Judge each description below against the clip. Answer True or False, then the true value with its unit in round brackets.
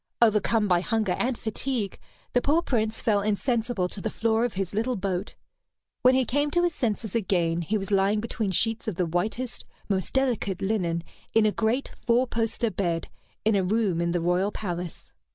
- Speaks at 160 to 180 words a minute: False (190 wpm)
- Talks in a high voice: True (215 Hz)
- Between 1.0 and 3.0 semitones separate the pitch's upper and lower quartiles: False (3.7 semitones)